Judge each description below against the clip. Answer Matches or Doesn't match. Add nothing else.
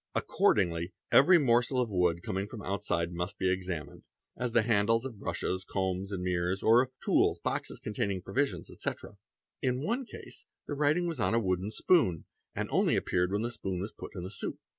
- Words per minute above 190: Matches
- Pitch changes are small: Doesn't match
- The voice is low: Matches